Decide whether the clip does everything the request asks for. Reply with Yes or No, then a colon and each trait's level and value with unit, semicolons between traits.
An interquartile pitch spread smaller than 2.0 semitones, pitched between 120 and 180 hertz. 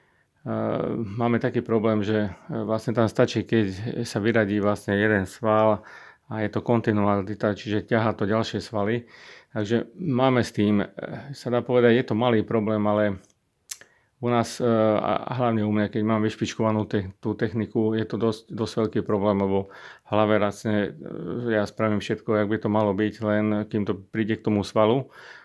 No: narrow, 1.5 semitones; low, 110 Hz